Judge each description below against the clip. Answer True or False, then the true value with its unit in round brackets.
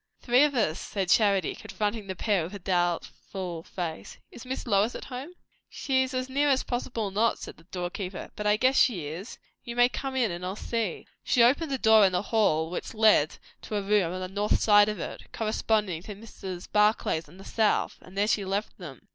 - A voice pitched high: True (210 Hz)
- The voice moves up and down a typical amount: True (4.2 semitones)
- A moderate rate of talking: False (215 wpm)